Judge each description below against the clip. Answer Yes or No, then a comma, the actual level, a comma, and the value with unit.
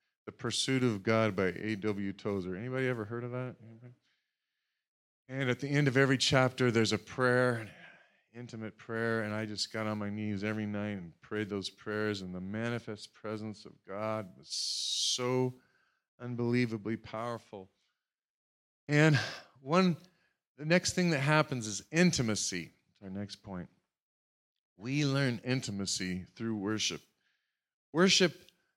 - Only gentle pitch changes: No, average, 3.5 semitones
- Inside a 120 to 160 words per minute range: Yes, average, 140 wpm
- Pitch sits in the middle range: No, low, 115 Hz